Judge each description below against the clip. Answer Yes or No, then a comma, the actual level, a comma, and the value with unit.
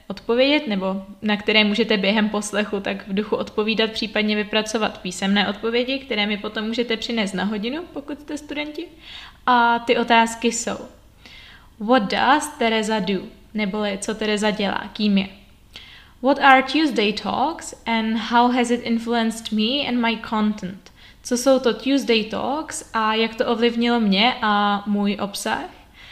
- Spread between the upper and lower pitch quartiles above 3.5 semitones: No, narrow, 2.6 semitones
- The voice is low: No, high, 225 Hz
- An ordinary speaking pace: Yes, average, 150 wpm